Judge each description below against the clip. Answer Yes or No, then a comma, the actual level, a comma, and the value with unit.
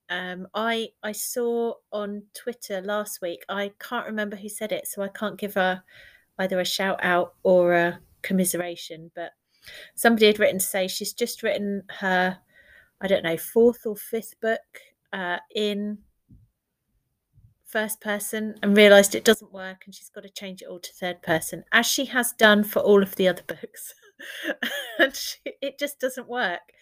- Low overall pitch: No, high, 205 Hz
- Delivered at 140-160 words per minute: No, average, 175 wpm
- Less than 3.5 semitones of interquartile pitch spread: Yes, average, 3.0 semitones